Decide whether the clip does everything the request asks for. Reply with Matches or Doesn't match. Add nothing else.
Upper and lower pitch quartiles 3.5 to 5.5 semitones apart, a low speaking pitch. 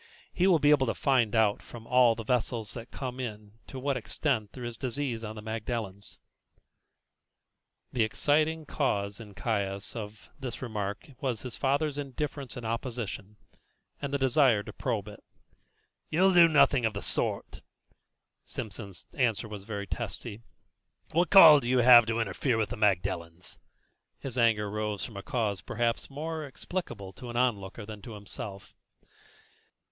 Matches